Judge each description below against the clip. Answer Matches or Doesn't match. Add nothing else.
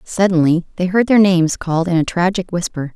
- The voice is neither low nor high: Matches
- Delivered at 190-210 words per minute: Matches